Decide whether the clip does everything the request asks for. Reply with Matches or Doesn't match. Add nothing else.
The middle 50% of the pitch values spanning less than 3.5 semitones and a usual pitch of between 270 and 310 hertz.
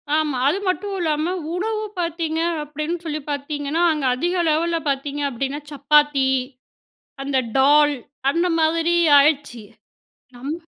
Matches